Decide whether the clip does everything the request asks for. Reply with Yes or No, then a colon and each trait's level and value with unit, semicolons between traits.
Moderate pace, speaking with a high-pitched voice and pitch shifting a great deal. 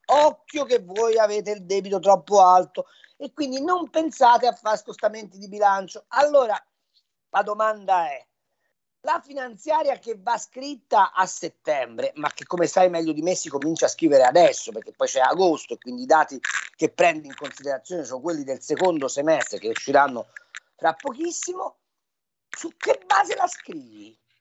Yes: average, 160 wpm; high, 220 Hz; wide, 9.0 semitones